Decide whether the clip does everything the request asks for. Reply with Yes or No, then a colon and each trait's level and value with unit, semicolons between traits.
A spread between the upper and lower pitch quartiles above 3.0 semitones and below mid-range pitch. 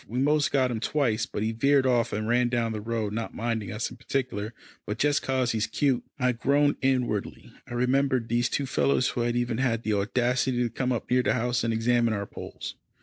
No: narrow, 2.4 semitones; low, 120 Hz